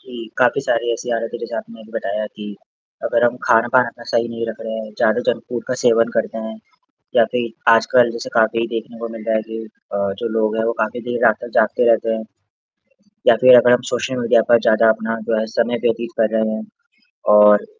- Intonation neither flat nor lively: No, narrow, 1.3 semitones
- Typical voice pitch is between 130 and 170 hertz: No, low, 115 Hz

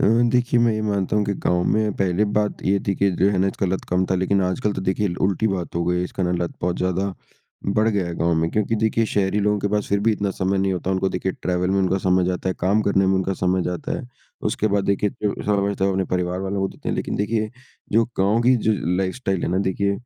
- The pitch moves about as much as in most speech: No, narrow, 2.1 semitones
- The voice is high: No, very low, 95 Hz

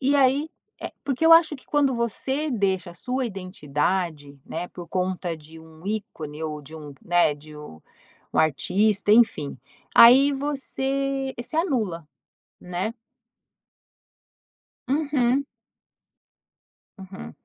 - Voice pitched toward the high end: Yes, high, 200 Hz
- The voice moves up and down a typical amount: No, wide, 9.0 semitones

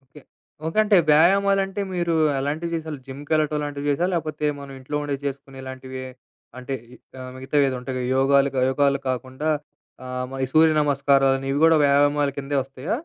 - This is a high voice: No, medium, 145 Hz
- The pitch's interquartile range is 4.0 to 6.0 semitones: No, average, 2.7 semitones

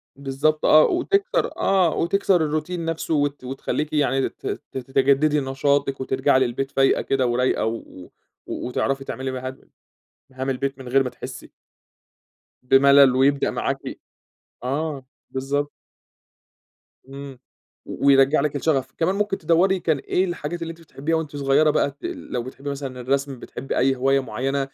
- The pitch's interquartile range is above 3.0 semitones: No, average, 2.7 semitones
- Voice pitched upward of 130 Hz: Yes, medium, 140 Hz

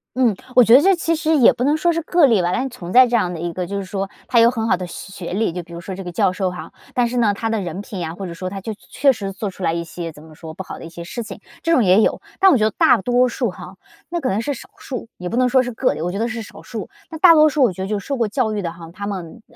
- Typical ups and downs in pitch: No, wide, 5.7 semitones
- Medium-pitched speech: No, high, 210 Hz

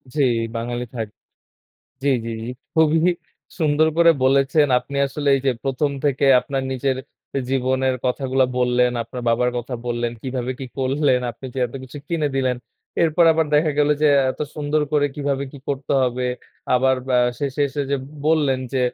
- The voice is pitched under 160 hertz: Yes, low, 135 Hz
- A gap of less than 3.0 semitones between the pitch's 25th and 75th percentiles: Yes, narrow, 2.5 semitones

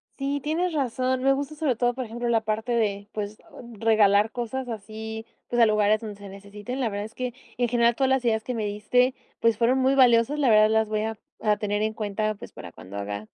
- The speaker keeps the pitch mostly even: No, average, 3.0 semitones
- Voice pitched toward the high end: Yes, high, 225 Hz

